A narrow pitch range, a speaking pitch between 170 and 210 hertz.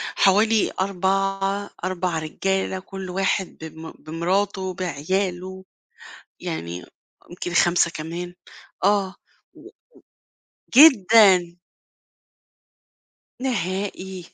Yes: narrow, 1.9 semitones; medium, 185 Hz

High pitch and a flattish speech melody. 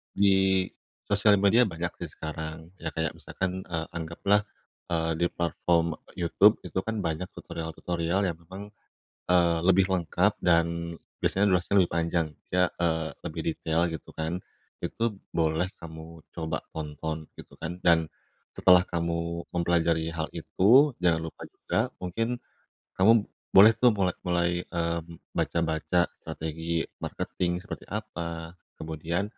No: very low, 85 Hz; narrow, 2.3 semitones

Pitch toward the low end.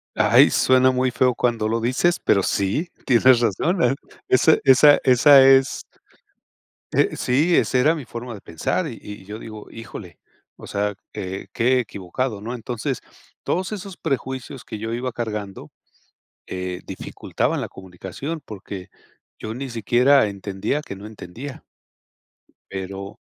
Yes: low, 120 Hz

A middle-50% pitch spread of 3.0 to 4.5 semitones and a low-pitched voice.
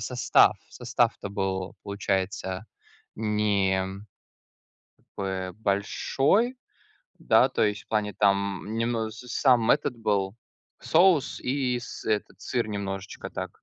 Yes: average, 3.4 semitones; low, 105 Hz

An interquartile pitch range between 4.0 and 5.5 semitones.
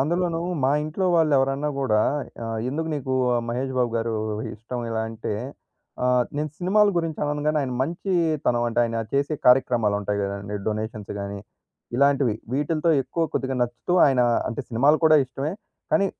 Yes: average, 5.0 semitones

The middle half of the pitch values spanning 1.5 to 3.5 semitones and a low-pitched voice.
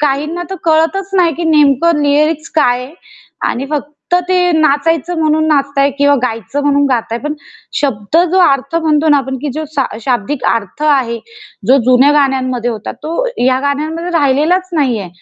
No: average, 3.1 semitones; very high, 290 Hz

